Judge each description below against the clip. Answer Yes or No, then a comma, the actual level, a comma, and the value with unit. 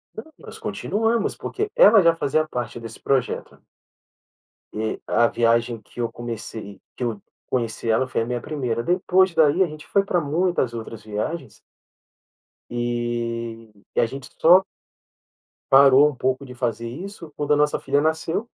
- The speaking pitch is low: Yes, low, 130 Hz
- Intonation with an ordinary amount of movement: No, wide, 5.7 semitones